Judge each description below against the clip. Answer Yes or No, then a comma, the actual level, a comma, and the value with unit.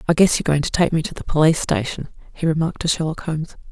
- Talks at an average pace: No, fast, 260 wpm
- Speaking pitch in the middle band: Yes, medium, 160 Hz